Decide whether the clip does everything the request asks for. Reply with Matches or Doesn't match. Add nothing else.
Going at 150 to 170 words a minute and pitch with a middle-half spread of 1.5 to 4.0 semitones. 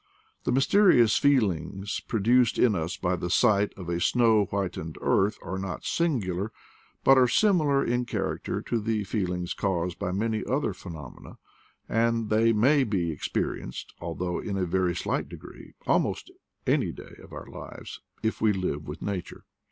Doesn't match